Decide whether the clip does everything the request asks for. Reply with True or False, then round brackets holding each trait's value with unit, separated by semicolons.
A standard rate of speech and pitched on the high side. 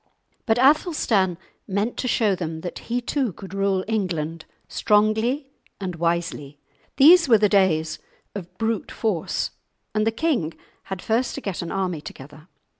True (150 wpm; 200 Hz)